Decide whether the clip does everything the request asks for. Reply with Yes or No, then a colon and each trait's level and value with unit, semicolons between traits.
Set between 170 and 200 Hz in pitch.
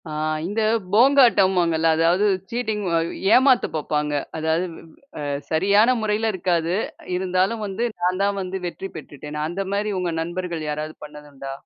Yes: medium, 185 Hz